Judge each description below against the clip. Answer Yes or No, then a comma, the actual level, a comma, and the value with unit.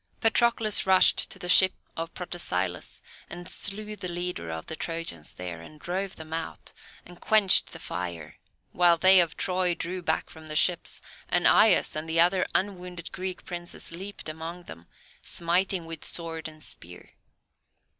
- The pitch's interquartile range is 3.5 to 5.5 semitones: No, average, 2.7 semitones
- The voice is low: No, medium, 175 Hz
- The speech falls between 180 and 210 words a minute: No, average, 160 wpm